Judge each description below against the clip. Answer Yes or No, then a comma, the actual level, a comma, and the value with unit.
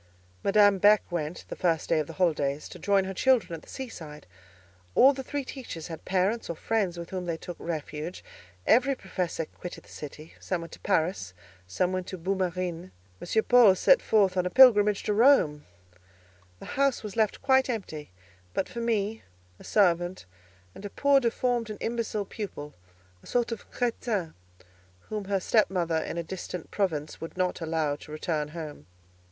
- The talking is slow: No, average, 180 wpm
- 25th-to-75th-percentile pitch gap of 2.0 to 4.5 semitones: No, average, 5.1 semitones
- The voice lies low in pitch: No, medium, 185 Hz